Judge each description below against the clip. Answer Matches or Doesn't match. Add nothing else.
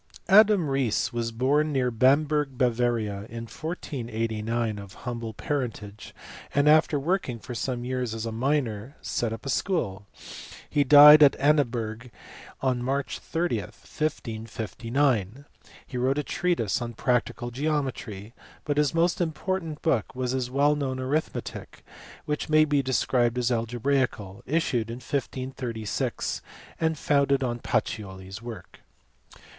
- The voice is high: Doesn't match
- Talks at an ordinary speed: Doesn't match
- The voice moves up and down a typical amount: Matches